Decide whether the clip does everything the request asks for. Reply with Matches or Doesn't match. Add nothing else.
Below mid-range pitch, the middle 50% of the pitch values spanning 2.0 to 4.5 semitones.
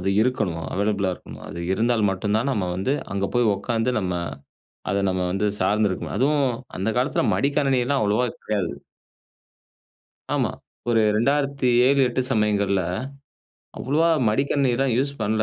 Doesn't match